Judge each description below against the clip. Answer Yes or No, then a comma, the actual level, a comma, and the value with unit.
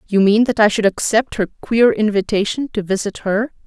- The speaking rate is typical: Yes, average, 195 wpm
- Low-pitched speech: No, high, 215 Hz